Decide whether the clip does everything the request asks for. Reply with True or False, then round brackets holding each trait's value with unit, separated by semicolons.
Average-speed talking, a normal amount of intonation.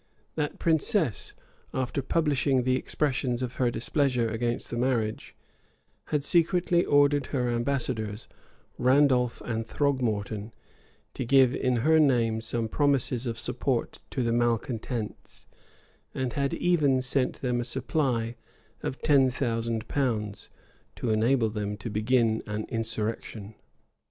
False (125 wpm; 3.3 semitones)